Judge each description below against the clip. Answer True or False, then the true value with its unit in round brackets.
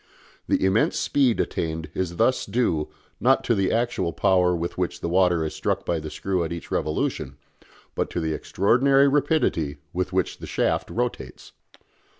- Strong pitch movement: True (6.4 semitones)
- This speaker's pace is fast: False (165 wpm)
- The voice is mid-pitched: False (90 Hz)